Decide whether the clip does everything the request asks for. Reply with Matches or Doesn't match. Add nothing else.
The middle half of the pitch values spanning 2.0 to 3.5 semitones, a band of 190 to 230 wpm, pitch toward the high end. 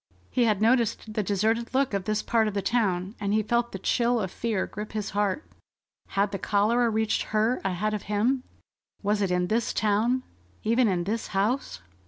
Matches